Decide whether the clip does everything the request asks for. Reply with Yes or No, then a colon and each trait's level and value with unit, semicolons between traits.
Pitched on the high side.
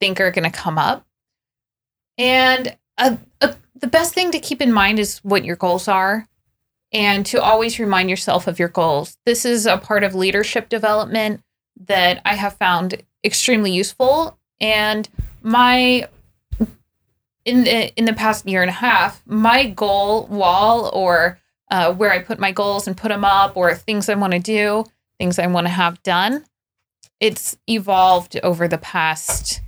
Yes: high, 205 Hz